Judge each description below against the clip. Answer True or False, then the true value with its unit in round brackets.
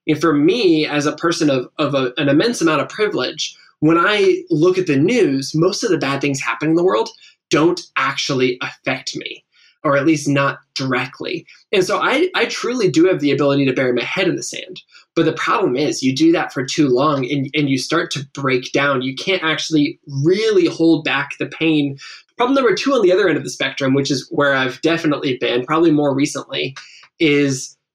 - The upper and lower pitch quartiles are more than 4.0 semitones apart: False (3.4 semitones)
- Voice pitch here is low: False (150 Hz)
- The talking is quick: True (215 wpm)